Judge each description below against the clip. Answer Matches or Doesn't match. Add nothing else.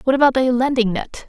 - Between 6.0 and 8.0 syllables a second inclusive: Matches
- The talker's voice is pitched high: Matches